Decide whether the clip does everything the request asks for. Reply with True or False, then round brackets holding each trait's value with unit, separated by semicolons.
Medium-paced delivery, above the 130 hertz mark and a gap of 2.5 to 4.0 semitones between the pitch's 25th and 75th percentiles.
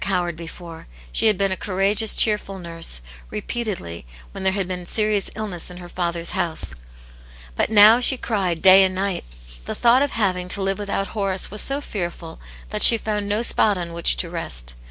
True (195 wpm; 190 Hz; 3.4 semitones)